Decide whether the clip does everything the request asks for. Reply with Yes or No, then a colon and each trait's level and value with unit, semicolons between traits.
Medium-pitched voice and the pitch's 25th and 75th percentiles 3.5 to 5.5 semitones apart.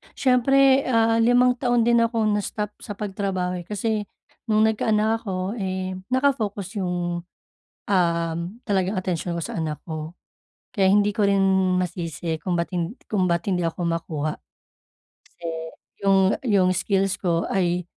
No: high, 195 Hz; average, 3.9 semitones